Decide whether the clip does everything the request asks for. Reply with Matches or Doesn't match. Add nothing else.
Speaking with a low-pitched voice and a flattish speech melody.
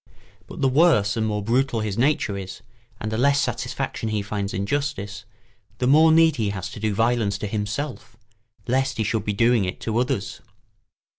Doesn't match